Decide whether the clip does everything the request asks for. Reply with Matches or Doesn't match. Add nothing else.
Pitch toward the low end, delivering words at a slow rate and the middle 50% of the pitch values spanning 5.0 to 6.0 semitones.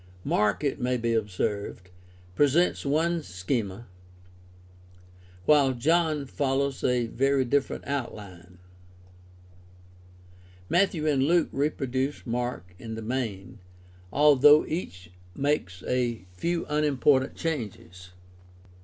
Matches